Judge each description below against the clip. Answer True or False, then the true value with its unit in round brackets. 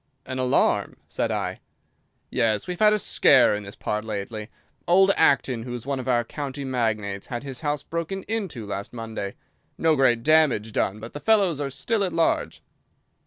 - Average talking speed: True (180 wpm)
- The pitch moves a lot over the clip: True (6.5 semitones)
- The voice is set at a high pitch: False (130 Hz)